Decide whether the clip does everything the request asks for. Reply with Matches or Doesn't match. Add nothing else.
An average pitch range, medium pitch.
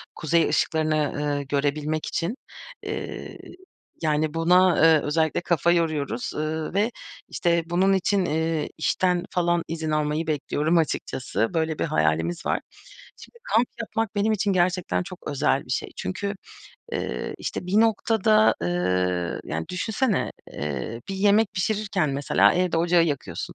Matches